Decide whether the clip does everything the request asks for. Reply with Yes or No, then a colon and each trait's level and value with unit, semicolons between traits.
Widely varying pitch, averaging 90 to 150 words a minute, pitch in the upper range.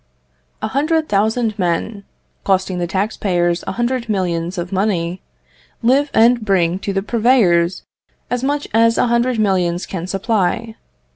No: average, 4.7 semitones; average, 145 wpm; high, 200 Hz